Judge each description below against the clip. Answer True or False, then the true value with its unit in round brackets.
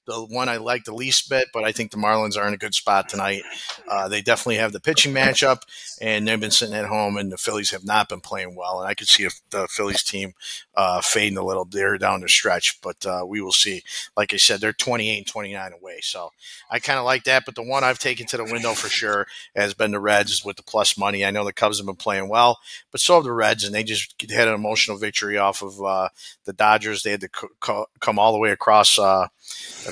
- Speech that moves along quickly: True (255 wpm)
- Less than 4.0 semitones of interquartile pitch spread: True (2.9 semitones)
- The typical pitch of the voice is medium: False (105 Hz)